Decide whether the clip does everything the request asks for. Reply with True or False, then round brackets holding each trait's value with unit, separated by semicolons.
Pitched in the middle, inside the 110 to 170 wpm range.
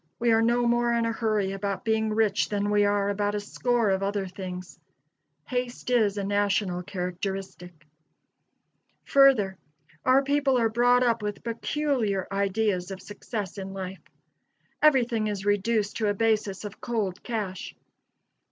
False (210 Hz; 150 wpm)